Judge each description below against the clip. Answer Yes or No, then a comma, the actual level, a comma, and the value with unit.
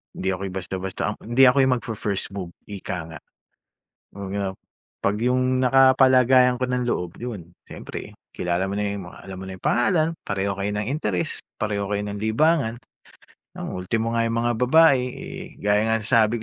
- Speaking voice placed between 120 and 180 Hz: No, low, 110 Hz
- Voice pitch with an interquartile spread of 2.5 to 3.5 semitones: No, average, 4.4 semitones